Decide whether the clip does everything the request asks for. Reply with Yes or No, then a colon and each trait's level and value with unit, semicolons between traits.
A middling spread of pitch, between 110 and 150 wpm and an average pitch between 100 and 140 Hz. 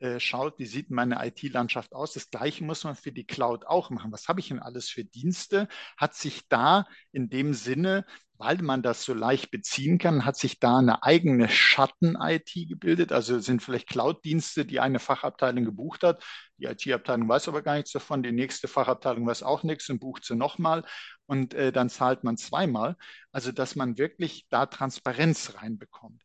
No: average, 3.9 semitones; average, 185 wpm; low, 135 Hz